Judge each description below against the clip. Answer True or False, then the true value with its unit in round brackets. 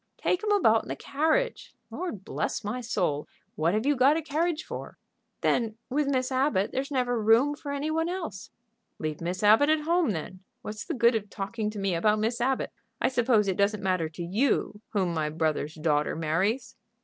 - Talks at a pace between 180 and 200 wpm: True (195 wpm)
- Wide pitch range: True (6.7 semitones)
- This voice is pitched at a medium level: False (225 Hz)